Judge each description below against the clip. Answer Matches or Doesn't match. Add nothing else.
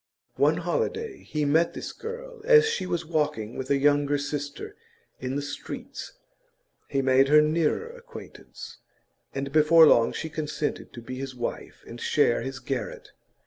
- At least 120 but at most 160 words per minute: Matches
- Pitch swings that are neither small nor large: Matches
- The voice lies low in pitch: Doesn't match